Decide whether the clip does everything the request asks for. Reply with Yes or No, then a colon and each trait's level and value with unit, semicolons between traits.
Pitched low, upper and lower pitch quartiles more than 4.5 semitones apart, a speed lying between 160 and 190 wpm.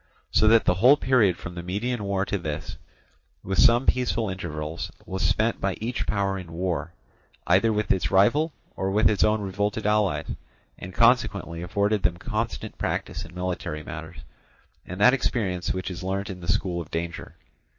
No: very low, 95 Hz; average, 3.3 semitones; average, 175 wpm